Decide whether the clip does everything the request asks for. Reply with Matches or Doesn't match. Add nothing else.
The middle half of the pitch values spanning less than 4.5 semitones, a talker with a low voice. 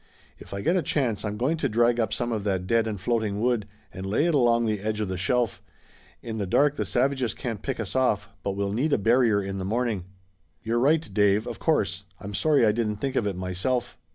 Matches